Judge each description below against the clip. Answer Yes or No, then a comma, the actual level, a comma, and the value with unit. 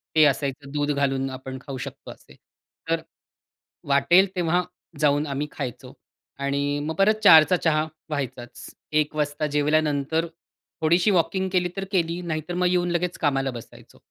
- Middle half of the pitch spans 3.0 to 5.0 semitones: Yes, average, 3.7 semitones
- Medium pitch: Yes, medium, 150 Hz